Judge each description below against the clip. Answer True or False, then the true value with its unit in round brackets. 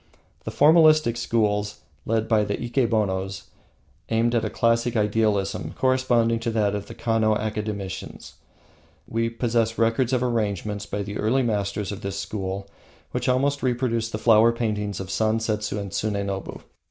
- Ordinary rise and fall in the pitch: False (2.3 semitones)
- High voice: False (110 Hz)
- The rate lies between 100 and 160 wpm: True (145 wpm)